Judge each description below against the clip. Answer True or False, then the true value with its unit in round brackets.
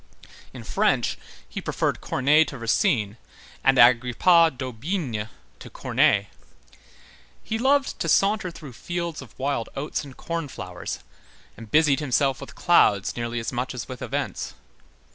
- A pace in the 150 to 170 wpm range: False (140 wpm)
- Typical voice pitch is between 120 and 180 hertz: True (135 Hz)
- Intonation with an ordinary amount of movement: False (5.9 semitones)